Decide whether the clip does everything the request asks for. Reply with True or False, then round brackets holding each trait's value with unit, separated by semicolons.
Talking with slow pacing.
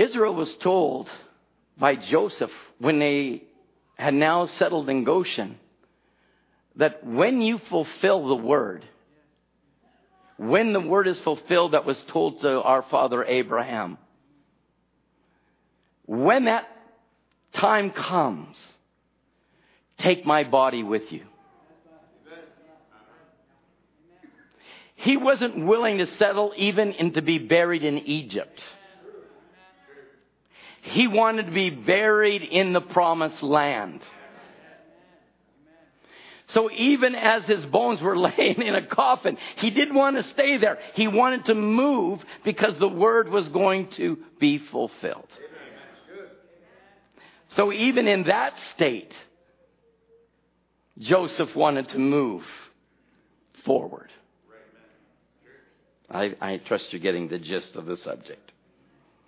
True (110 wpm)